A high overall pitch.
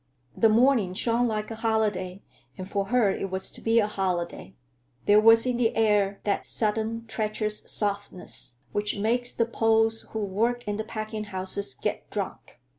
Yes: high, 215 Hz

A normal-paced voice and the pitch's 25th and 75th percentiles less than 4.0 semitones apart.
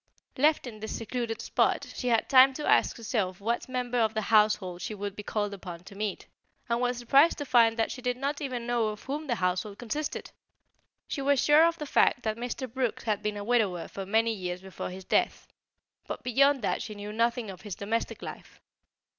No: fast, 215 wpm; average, 3.5 semitones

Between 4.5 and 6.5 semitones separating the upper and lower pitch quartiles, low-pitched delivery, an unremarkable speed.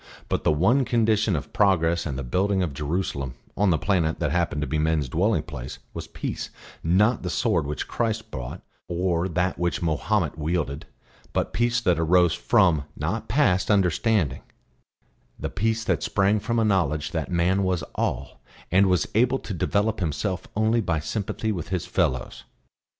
Yes: average, 4.8 semitones; very low, 90 Hz; average, 170 wpm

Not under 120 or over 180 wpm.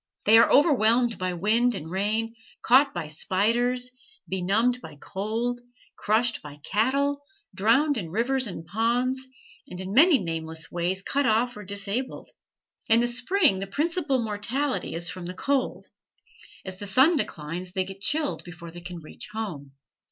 Yes: average, 155 wpm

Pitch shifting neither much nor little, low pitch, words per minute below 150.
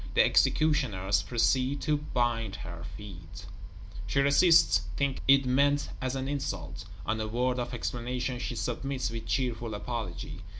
Yes: average, 4.0 semitones; low, 125 Hz; average, 140 wpm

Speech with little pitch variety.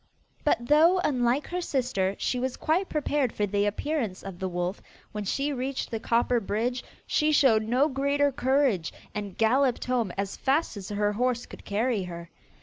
No: average, 5.3 semitones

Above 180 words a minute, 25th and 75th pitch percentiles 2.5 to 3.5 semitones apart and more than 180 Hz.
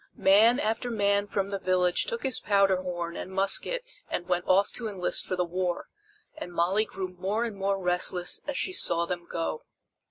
Yes: average, 190 wpm; average, 2.9 semitones; high, 190 Hz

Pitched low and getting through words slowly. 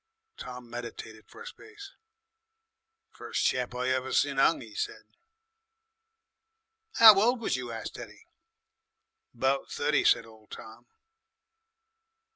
Yes: low, 130 Hz; slow, 115 wpm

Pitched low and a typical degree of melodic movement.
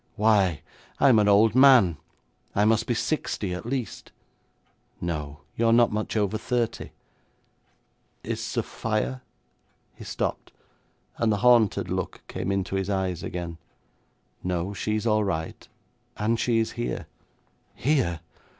Yes: low, 105 Hz; average, 4.1 semitones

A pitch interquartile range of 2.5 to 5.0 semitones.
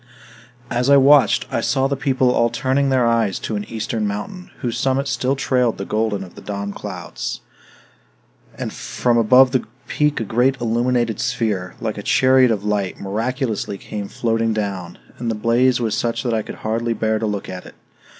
Yes: average, 3.4 semitones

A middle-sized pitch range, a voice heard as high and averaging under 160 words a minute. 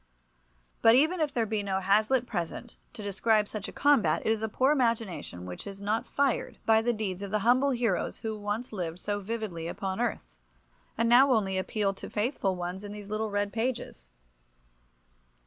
No: average, 3.1 semitones; high, 215 Hz; average, 185 wpm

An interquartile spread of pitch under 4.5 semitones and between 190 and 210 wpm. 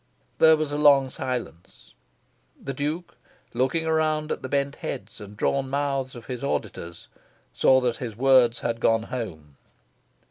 No: average, 3.7 semitones; average, 150 wpm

